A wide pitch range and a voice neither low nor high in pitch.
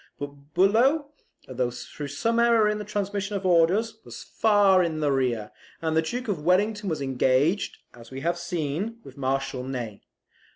Yes: wide, 7.3 semitones; medium, 170 Hz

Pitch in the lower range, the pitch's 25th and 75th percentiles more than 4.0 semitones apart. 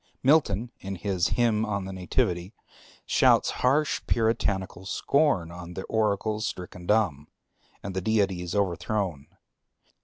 No: low, 100 Hz; average, 3.6 semitones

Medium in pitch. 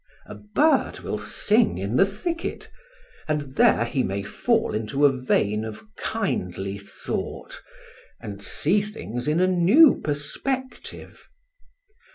Yes: medium, 150 Hz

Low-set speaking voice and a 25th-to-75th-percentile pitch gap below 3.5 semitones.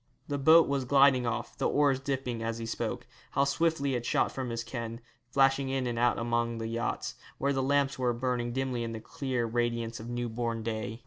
Yes: low, 120 Hz; narrow, 2.6 semitones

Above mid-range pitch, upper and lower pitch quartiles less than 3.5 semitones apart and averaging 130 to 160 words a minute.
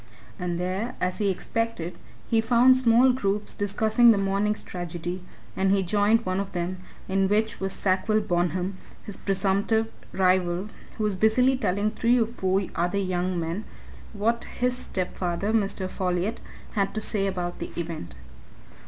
Yes: high, 195 Hz; average, 3.1 semitones; average, 155 wpm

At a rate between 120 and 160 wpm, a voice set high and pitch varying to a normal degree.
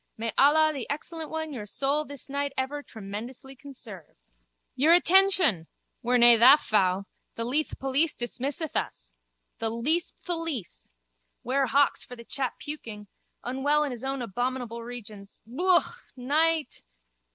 Yes: slow, 135 wpm; very high, 265 Hz; average, 4.4 semitones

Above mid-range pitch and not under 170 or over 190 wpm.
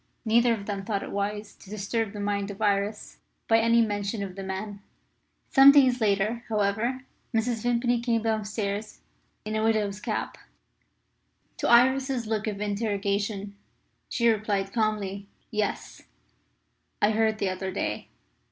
No: high, 215 Hz; average, 145 wpm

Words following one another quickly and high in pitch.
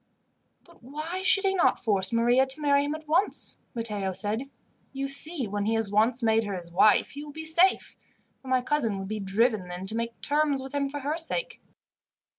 Yes: fast, 210 wpm; very high, 255 Hz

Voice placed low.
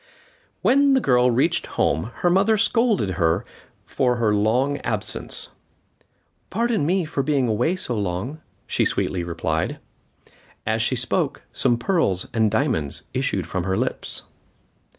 Yes: low, 125 Hz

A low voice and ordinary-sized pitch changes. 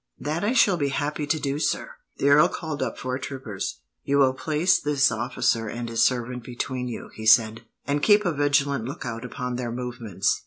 Yes: low, 130 Hz; average, 3.5 semitones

